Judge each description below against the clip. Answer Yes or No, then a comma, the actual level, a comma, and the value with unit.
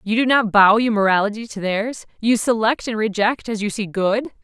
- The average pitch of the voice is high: Yes, high, 220 Hz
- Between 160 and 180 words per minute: No, fast, 205 wpm